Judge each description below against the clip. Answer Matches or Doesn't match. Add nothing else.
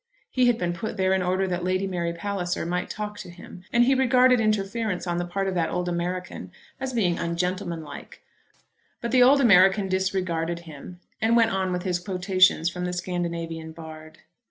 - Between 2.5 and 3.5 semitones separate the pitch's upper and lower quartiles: Matches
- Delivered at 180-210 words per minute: Matches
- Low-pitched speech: Doesn't match